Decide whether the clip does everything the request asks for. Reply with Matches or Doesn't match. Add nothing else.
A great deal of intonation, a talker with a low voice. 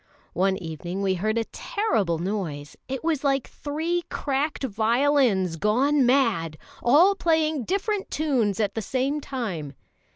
Doesn't match